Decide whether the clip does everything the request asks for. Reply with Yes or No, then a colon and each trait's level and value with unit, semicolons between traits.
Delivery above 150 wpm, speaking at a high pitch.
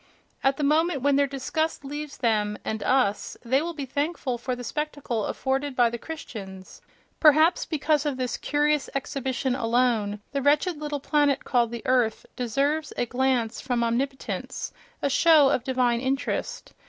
Yes: average, 160 wpm; very high, 270 Hz